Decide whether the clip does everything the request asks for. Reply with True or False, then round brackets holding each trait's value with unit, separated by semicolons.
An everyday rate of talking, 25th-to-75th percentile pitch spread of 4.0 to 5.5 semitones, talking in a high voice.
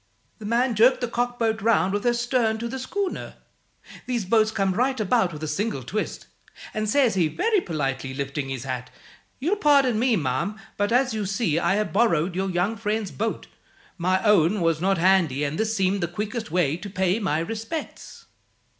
True (190 wpm; 5.2 semitones; 205 Hz)